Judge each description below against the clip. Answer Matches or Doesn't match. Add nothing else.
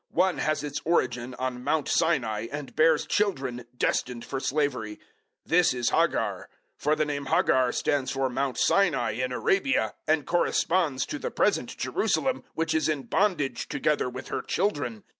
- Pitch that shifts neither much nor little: Matches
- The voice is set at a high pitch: Doesn't match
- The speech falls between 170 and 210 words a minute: Doesn't match